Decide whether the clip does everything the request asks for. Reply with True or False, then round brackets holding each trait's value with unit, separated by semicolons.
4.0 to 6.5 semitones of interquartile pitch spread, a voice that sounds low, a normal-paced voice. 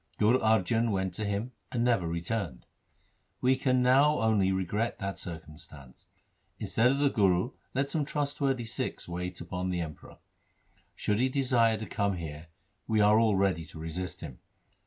True (5.6 semitones; 105 Hz; 165 wpm)